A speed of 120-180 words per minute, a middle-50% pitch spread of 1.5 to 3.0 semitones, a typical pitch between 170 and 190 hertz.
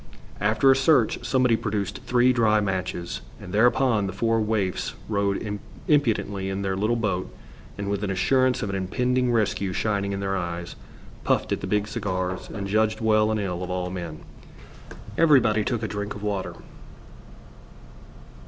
No: average, 160 wpm; average, 2.7 semitones; low, 105 Hz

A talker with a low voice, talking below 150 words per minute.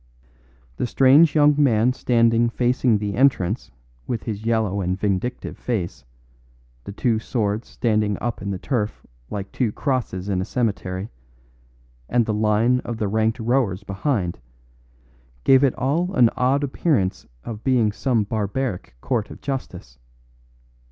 Yes: low, 115 Hz; average, 140 wpm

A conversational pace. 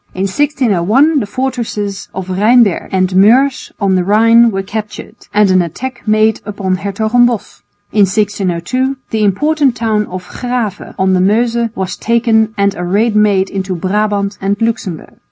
Yes: average, 155 wpm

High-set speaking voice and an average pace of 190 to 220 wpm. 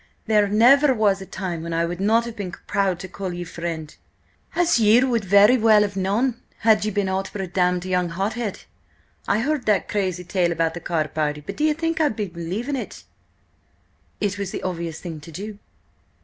Yes: high, 195 Hz; fast, 205 wpm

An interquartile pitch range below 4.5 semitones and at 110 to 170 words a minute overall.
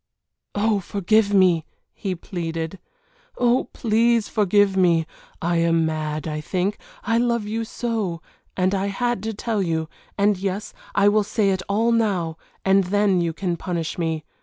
Yes: average, 4.0 semitones; average, 160 wpm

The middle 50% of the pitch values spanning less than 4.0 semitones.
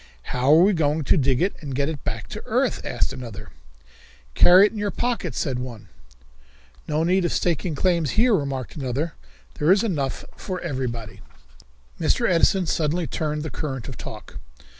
No: average, 5.2 semitones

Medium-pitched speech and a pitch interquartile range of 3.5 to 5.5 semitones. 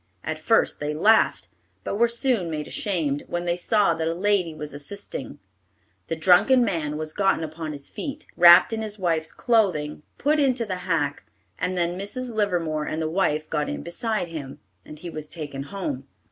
Yes: medium, 175 Hz; average, 5.1 semitones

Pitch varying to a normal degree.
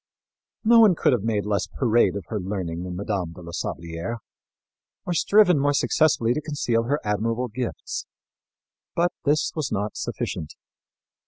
No: wide, 6.8 semitones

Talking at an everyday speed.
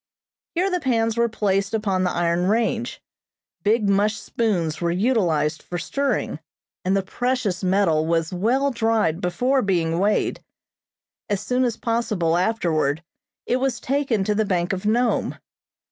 Yes: average, 145 wpm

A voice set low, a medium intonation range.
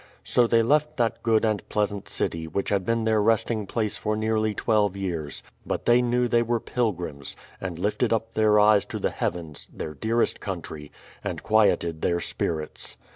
Yes: low, 105 Hz; average, 4.1 semitones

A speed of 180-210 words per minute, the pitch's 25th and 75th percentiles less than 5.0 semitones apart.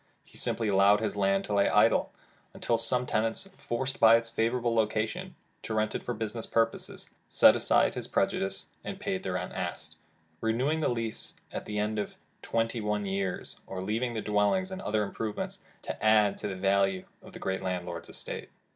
Yes: average, 185 wpm; average, 2.7 semitones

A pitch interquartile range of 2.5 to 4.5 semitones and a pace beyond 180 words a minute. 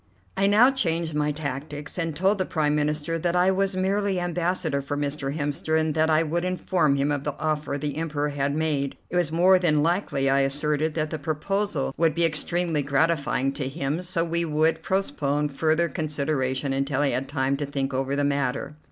Yes: average, 3.1 semitones; average, 195 wpm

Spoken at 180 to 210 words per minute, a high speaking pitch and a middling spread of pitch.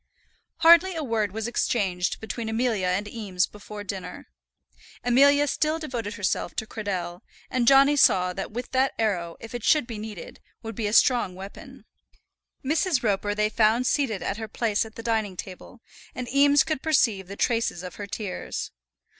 No: average, 170 wpm; high, 220 Hz; average, 4.1 semitones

